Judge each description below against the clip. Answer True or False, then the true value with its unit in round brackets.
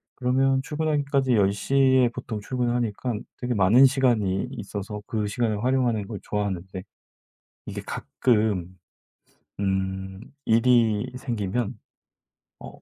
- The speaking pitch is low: True (115 Hz)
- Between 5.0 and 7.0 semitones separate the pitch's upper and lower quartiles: False (4.0 semitones)